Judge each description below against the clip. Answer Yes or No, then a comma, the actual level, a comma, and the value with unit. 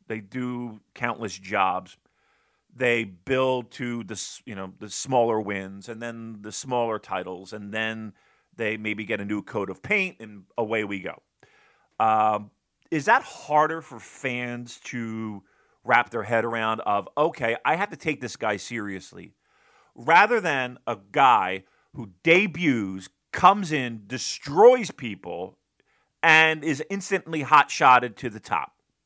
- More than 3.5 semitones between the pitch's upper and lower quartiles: Yes, average, 3.9 semitones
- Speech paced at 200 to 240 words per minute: No, average, 145 wpm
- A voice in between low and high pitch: No, low, 115 Hz